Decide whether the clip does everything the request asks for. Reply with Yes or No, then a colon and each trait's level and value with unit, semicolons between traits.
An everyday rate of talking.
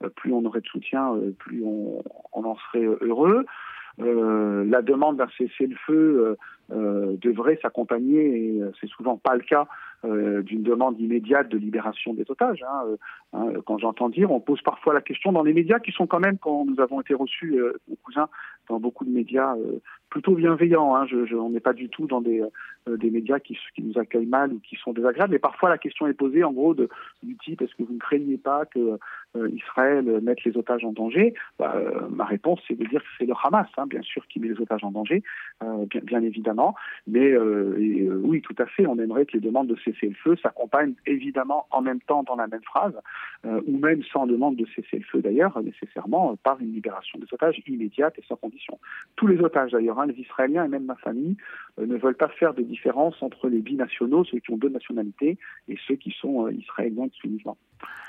No: fast, 230 wpm